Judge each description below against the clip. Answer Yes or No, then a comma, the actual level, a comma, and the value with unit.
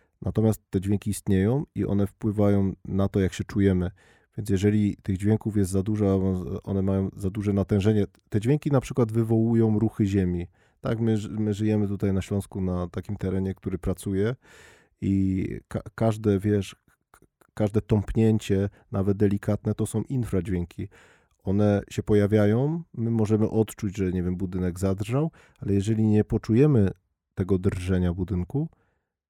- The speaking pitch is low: Yes, low, 100 Hz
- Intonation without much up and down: Yes, narrow, 2.2 semitones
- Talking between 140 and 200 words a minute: Yes, average, 145 wpm